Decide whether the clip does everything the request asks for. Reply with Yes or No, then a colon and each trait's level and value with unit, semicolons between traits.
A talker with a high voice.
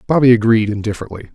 No: low, 115 Hz